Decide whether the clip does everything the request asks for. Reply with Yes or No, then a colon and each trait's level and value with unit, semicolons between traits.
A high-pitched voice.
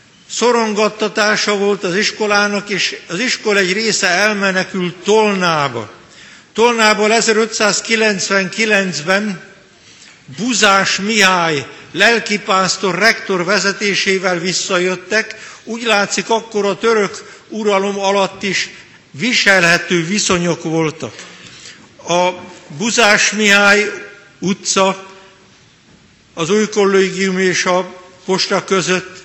Yes: high, 195 Hz